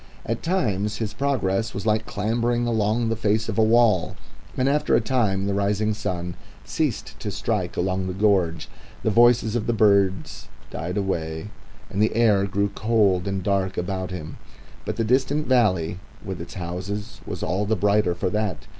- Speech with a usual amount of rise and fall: Yes, average, 3.1 semitones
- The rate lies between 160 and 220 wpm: Yes, average, 180 wpm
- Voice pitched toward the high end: No, low, 105 Hz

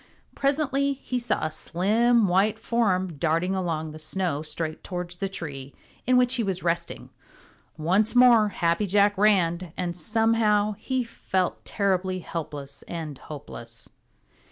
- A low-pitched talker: No, medium, 185 Hz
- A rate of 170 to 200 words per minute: No, slow, 135 wpm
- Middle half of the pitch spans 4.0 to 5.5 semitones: Yes, average, 4.6 semitones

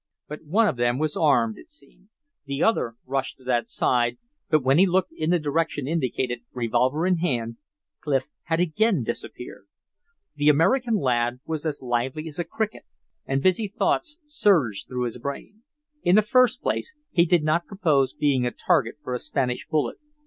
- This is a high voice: No, medium, 150 Hz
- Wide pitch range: Yes, wide, 5.9 semitones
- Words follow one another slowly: No, average, 180 wpm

